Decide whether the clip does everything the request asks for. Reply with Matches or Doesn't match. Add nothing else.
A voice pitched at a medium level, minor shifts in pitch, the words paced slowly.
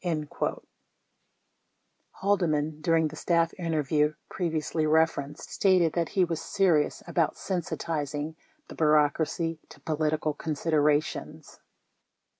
Matches